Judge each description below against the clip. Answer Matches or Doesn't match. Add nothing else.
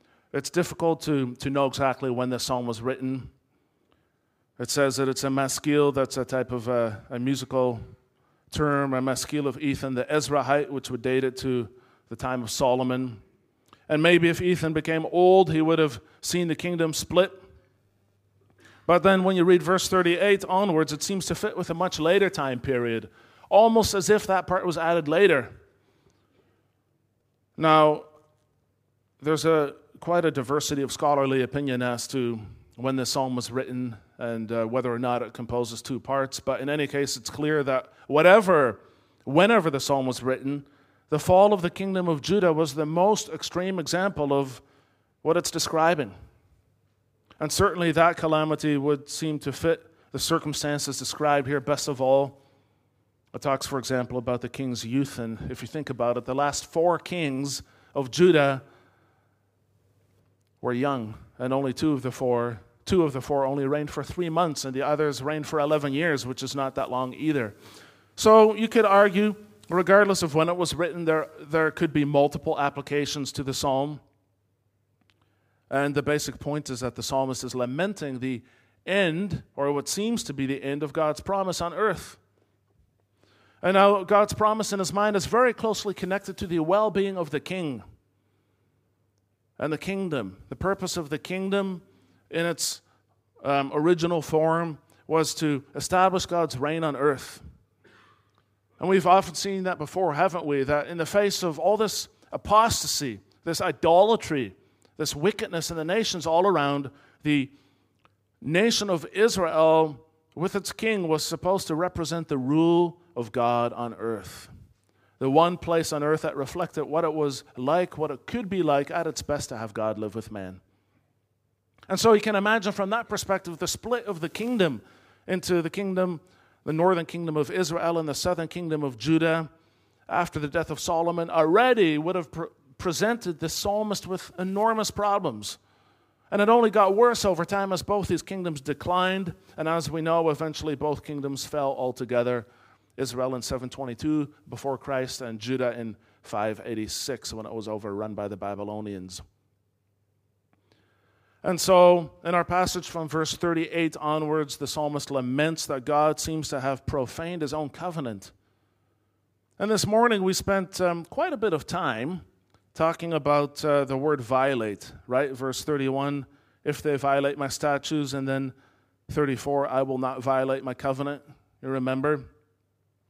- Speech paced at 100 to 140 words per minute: Doesn't match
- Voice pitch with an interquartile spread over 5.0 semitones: Matches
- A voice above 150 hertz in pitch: Doesn't match